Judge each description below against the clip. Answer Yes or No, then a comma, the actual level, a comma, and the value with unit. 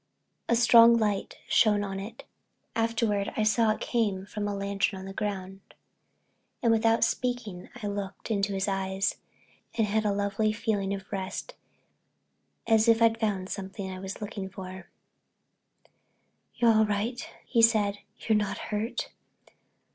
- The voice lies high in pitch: Yes, high, 205 Hz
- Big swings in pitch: No, narrow, 2.5 semitones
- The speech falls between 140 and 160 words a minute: Yes, average, 145 wpm